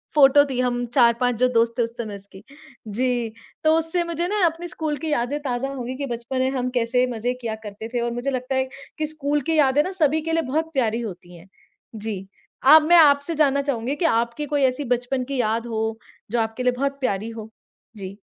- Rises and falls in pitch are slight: No, average, 3.9 semitones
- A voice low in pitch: No, very high, 255 Hz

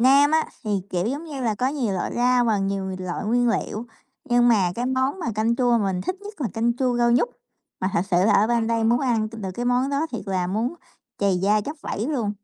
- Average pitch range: Yes, average, 3.8 semitones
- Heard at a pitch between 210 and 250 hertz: Yes, high, 235 Hz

